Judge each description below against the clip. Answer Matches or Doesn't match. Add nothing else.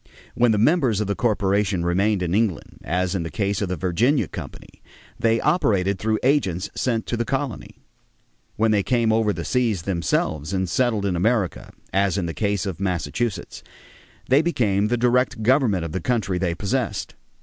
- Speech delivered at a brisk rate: Doesn't match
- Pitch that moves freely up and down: Doesn't match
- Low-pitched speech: Matches